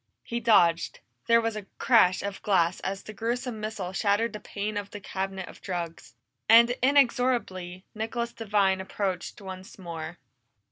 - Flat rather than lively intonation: No, average, 3.4 semitones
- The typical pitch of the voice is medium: No, high, 200 Hz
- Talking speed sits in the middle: Yes, average, 150 wpm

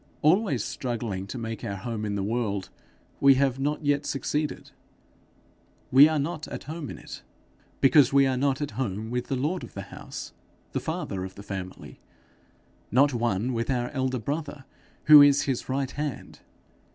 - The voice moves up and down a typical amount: Yes, average, 4.0 semitones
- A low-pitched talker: Yes, low, 130 Hz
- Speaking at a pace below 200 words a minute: Yes, average, 175 wpm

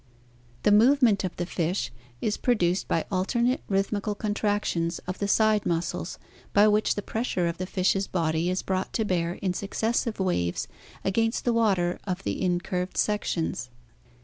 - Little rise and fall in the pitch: No, average, 3.2 semitones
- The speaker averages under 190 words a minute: Yes, average, 165 wpm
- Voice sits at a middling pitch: No, high, 195 Hz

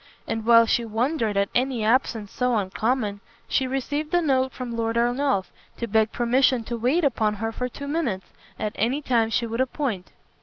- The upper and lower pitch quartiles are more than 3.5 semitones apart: No, average, 3.0 semitones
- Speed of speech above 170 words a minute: Yes, average, 185 wpm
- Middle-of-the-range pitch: No, high, 235 Hz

